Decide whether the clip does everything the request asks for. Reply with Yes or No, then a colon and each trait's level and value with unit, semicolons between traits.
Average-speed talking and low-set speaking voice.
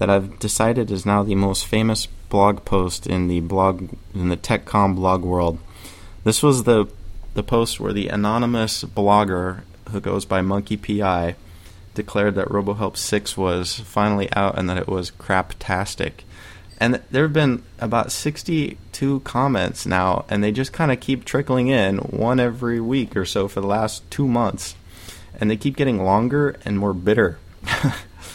Yes: average, 165 wpm; low, 100 Hz